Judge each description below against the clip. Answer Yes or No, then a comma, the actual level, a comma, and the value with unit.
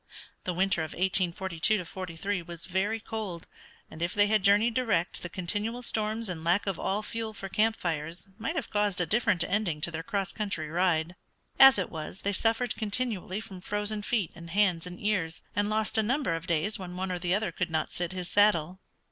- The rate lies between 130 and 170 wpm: No, fast, 205 wpm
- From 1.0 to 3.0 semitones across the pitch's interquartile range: No, average, 3.6 semitones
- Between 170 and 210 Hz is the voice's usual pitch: Yes, high, 190 Hz